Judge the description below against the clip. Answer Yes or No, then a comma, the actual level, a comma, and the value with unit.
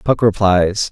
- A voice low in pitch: Yes, low, 100 Hz